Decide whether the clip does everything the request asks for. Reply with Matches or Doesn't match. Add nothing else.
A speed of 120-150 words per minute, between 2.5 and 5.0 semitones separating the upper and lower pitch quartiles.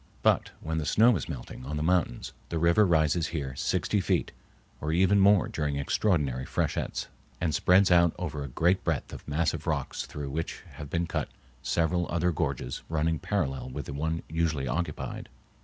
Doesn't match